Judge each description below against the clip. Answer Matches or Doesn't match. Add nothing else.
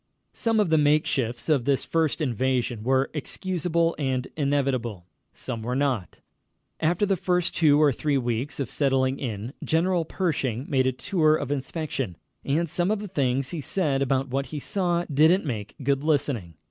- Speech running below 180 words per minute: Matches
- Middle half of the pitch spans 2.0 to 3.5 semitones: Doesn't match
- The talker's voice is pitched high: Doesn't match